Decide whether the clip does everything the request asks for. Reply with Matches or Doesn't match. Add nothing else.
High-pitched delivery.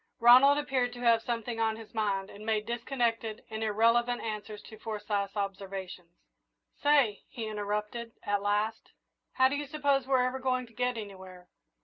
Matches